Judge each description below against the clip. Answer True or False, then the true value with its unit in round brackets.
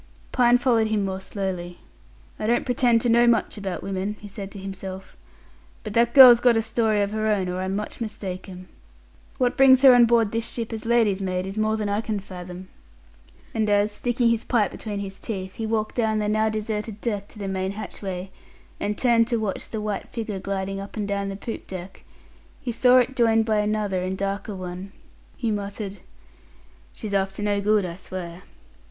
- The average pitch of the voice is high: True (210 Hz)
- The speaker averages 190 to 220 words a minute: True (200 wpm)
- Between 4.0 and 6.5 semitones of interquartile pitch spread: False (2.9 semitones)